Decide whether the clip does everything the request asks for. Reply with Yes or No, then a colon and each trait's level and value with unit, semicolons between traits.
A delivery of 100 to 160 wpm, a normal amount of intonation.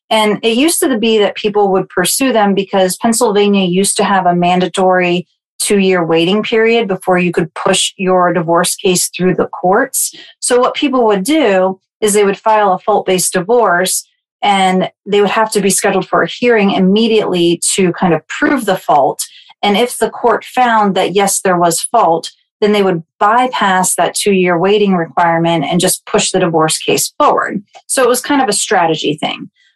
No: average, 190 wpm; average, 3.4 semitones